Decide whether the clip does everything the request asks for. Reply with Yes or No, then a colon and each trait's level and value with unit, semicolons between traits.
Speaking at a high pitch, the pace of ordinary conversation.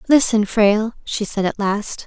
Yes: high, 220 Hz; average, 175 wpm